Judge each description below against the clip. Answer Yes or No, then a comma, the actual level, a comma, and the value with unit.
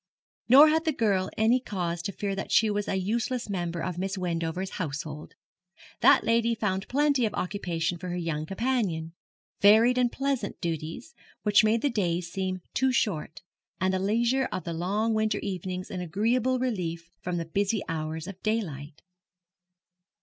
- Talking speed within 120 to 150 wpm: No, average, 165 wpm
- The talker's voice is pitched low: No, high, 195 Hz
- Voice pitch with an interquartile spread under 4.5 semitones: No, average, 4.9 semitones